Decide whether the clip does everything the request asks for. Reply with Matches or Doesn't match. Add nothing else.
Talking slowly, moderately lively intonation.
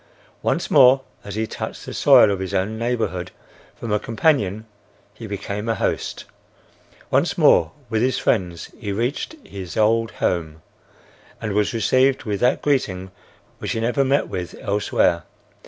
Doesn't match